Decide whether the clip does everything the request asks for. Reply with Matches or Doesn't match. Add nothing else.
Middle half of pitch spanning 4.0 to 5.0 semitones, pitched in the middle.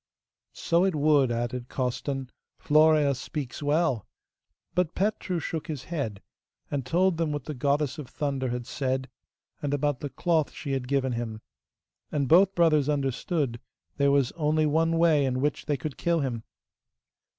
Doesn't match